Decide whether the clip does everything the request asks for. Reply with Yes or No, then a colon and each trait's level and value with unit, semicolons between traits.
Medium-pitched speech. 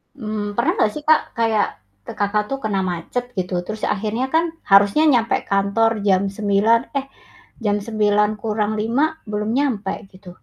No: high, 215 Hz